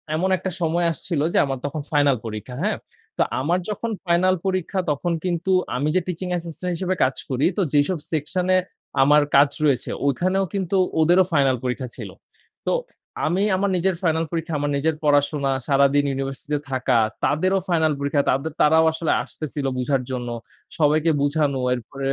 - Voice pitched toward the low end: No, medium, 155 Hz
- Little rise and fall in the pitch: No, average, 4.0 semitones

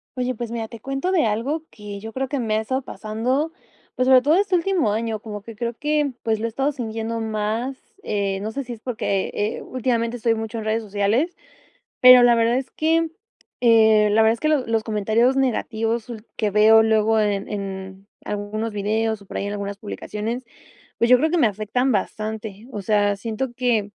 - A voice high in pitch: Yes, high, 225 Hz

